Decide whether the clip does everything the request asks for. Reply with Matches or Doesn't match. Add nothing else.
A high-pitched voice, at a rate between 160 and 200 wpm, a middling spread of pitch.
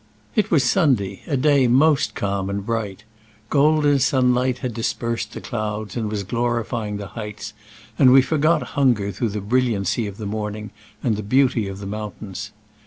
Doesn't match